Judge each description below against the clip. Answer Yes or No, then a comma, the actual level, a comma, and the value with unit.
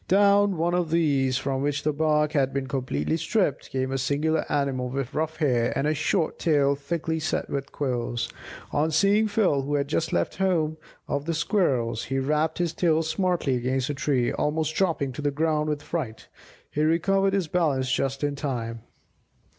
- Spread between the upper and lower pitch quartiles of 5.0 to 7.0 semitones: No, average, 3.3 semitones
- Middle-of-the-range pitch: Yes, medium, 150 Hz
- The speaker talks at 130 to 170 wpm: No, average, 185 wpm